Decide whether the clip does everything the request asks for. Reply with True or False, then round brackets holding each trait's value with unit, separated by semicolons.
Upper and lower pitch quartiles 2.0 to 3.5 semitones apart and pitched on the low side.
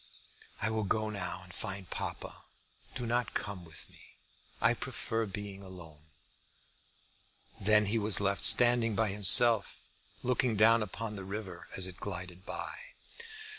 True (3.1 semitones; 100 Hz)